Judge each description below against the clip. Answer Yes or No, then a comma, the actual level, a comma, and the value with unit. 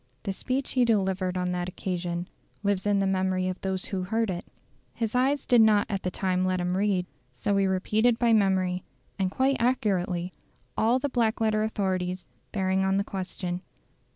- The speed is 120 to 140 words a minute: No, average, 180 wpm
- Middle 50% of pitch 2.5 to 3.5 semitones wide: Yes, average, 3.0 semitones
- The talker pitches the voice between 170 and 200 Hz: Yes, high, 190 Hz